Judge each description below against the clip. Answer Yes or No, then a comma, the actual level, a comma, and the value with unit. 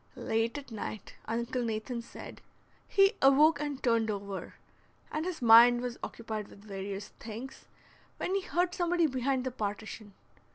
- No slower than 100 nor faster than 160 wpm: Yes, average, 150 wpm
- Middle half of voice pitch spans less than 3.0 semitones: No, average, 4.6 semitones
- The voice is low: No, high, 240 Hz